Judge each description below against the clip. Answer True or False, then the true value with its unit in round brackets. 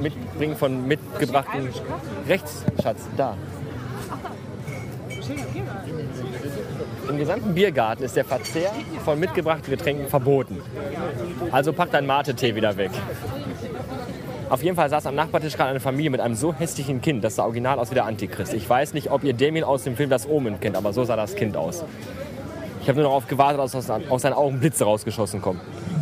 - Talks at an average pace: True (165 wpm)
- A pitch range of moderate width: True (3.3 semitones)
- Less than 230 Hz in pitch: True (135 Hz)